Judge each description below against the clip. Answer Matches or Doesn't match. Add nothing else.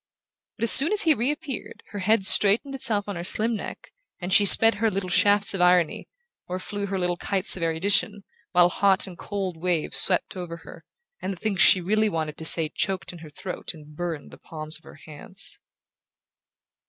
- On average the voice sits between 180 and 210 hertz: Matches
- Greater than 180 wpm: Matches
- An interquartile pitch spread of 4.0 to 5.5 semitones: Doesn't match